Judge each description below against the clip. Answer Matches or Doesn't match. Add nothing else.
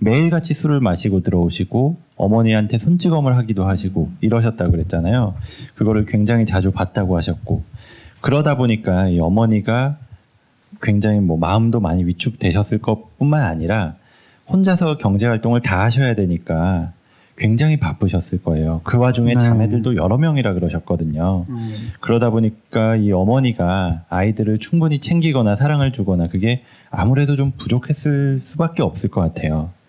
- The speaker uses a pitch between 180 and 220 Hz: Doesn't match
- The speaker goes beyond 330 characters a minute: Matches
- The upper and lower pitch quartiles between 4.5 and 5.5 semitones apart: Matches